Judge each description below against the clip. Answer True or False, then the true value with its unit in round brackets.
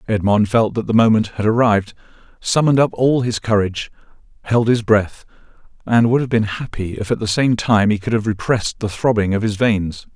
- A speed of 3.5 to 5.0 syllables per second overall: False (5.5 syllables/s)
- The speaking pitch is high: False (110 Hz)